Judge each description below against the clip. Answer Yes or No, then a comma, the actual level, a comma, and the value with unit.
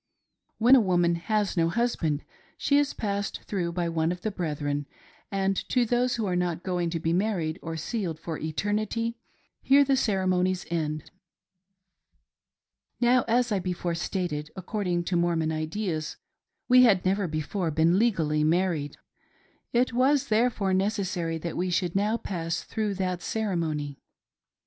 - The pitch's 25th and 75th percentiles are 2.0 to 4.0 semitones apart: No, average, 4.6 semitones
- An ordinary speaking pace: Yes, average, 150 wpm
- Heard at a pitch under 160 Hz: No, medium, 185 Hz